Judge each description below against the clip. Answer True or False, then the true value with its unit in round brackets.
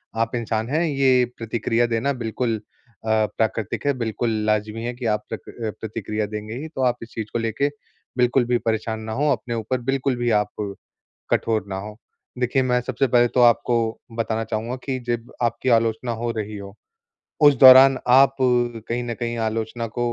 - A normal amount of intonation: False (2.2 semitones)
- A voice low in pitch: True (120 Hz)